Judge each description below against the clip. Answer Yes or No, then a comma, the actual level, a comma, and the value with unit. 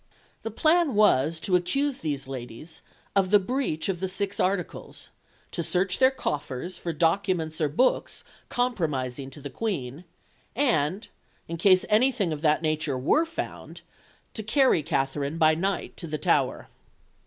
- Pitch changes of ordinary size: No, wide, 5.8 semitones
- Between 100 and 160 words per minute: Yes, average, 150 wpm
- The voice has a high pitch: No, medium, 175 Hz